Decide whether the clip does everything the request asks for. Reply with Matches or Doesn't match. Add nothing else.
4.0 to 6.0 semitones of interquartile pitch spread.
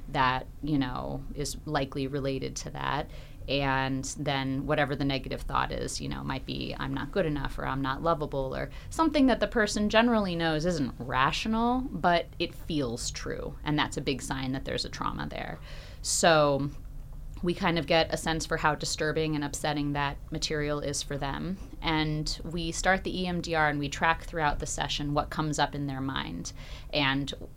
Doesn't match